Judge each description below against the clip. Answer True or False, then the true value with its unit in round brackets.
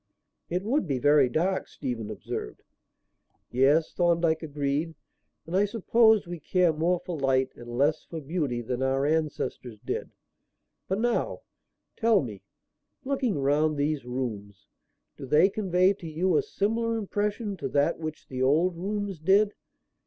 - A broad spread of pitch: True (5.9 semitones)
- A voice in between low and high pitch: True (160 Hz)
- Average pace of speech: True (145 wpm)